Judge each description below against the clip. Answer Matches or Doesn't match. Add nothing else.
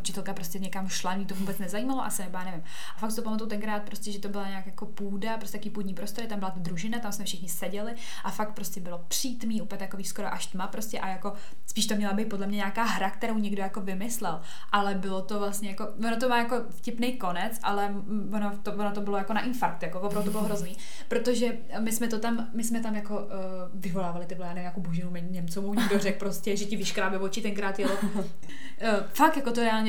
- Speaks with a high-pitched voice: Matches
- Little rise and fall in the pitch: Matches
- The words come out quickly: Matches